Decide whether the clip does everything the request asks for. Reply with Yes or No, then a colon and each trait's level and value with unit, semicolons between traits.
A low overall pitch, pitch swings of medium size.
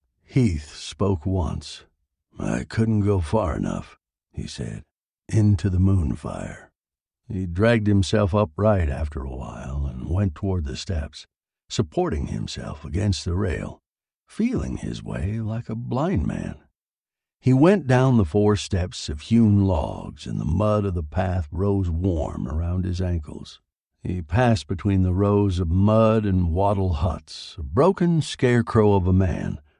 Yes: very low, 95 Hz; average, 4.1 semitones